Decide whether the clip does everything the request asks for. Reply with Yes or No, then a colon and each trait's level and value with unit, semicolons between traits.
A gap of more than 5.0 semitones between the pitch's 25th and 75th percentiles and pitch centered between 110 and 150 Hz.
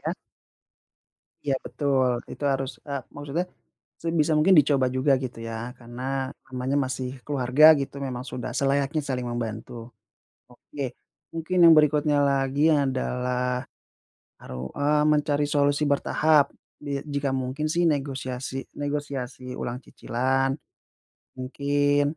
No: narrow, 2.4 semitones; medium, 140 Hz